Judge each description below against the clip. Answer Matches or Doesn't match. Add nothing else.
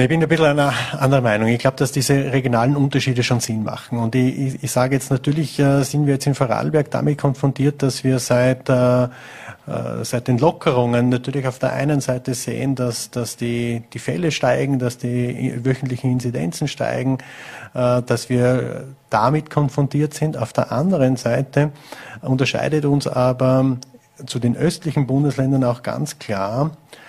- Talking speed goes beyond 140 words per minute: Matches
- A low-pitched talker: Matches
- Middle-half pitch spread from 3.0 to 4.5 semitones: Doesn't match